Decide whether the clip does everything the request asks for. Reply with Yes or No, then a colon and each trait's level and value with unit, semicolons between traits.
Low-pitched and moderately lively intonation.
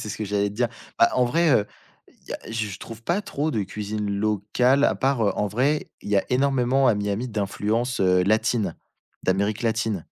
Yes: low, 110 Hz; average, 3.6 semitones